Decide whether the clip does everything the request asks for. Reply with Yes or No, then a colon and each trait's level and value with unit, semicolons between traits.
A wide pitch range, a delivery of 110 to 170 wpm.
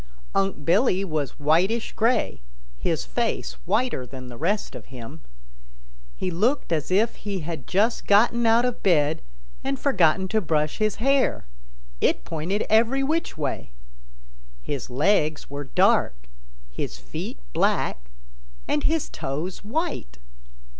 Yes: wide, 7.6 semitones; slow, 135 wpm